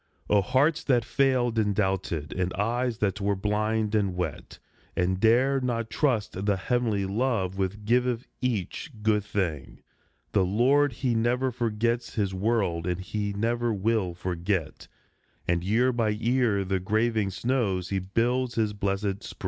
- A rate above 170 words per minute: No, average, 155 wpm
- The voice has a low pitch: Yes, low, 105 Hz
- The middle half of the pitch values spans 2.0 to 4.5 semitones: Yes, average, 3.7 semitones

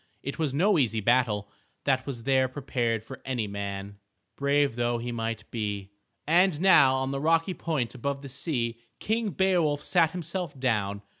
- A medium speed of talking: Yes, average, 165 wpm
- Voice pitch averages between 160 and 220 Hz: No, low, 130 Hz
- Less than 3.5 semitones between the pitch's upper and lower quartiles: No, average, 5.3 semitones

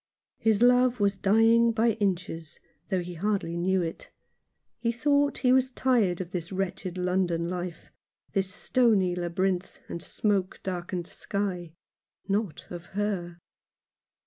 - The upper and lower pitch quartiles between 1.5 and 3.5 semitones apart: No, average, 4.0 semitones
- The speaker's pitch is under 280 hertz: Yes, high, 190 Hz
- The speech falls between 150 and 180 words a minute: No, average, 140 wpm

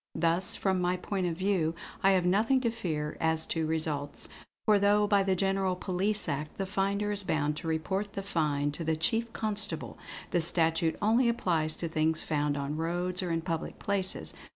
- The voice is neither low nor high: Yes, medium, 180 Hz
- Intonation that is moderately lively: Yes, average, 3.8 semitones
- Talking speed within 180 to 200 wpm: Yes, average, 190 wpm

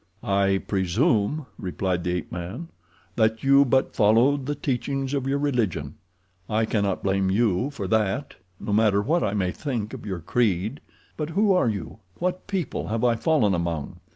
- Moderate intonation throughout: No, wide, 6.0 semitones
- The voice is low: Yes, low, 110 Hz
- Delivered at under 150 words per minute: No, average, 165 wpm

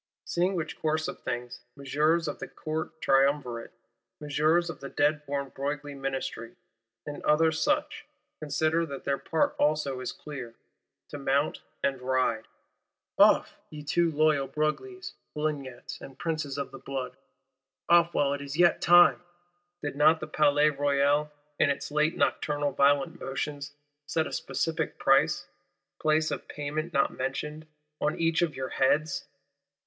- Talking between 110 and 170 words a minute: Yes, average, 145 wpm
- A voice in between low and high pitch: Yes, medium, 145 Hz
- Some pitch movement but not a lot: No, narrow, 2.2 semitones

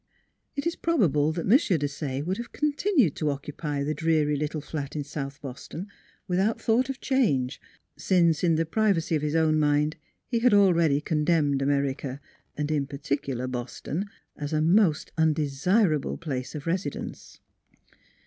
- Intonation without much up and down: No, average, 4.4 semitones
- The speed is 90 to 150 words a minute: No, average, 160 wpm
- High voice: No, medium, 155 Hz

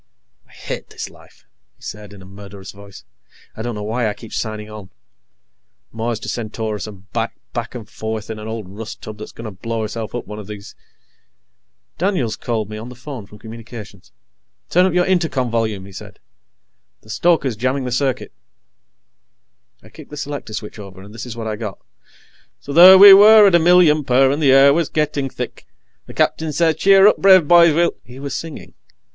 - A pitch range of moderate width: No, wide, 5.7 semitones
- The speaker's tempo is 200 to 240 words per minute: Yes, fast, 205 wpm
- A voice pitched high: No, low, 115 Hz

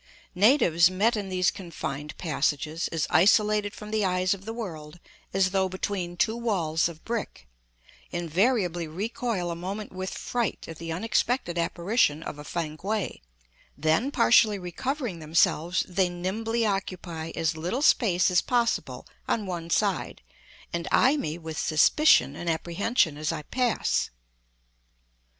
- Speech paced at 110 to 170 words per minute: Yes, average, 140 wpm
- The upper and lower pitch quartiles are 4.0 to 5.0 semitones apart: Yes, average, 4.6 semitones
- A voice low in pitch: No, medium, 185 Hz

